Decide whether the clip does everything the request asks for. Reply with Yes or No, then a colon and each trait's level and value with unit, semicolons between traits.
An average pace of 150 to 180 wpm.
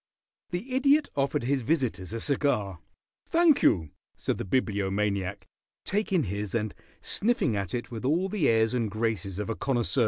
Yes: average, 160 wpm